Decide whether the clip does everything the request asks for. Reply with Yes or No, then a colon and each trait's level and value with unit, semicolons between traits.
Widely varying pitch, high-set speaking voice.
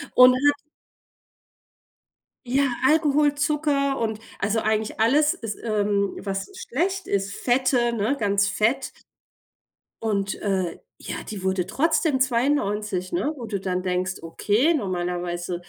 Yes: wide, 6.1 semitones; high, 220 Hz